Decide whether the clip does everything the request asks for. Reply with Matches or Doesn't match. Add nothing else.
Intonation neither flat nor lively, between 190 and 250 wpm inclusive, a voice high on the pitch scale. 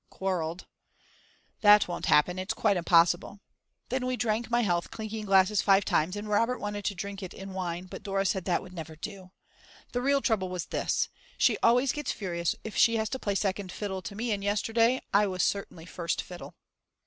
Matches